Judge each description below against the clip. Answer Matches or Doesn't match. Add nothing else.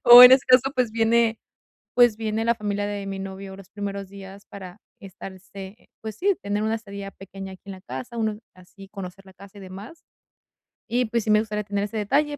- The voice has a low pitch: Doesn't match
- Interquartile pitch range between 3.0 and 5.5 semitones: Doesn't match